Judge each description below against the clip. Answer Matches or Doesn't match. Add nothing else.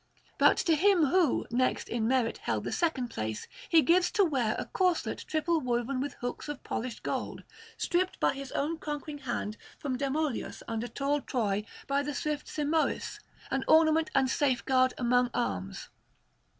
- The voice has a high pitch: Matches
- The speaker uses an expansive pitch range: Doesn't match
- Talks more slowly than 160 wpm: Doesn't match